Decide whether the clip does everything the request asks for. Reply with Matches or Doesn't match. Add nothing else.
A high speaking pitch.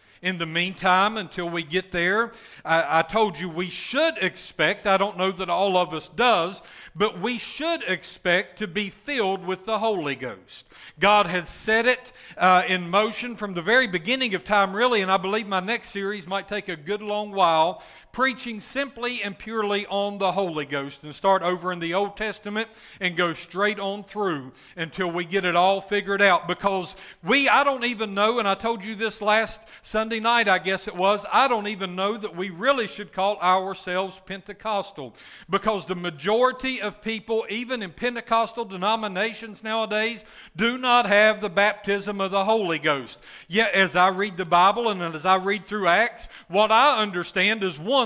Matches